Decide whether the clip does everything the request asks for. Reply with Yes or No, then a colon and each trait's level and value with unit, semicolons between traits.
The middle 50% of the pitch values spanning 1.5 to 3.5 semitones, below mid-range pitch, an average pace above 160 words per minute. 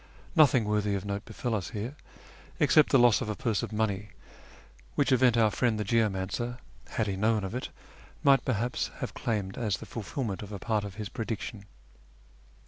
Yes: average, 2.9 semitones; low, 110 Hz; average, 185 wpm